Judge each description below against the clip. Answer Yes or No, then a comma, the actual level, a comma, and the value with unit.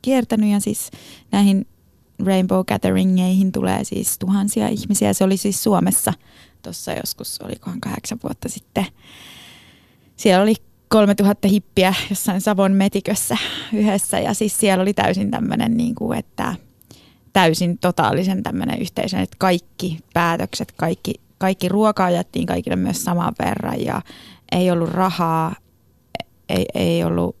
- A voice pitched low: No, high, 195 Hz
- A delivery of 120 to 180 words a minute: Yes, average, 130 wpm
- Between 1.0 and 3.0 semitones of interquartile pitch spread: Yes, average, 2.7 semitones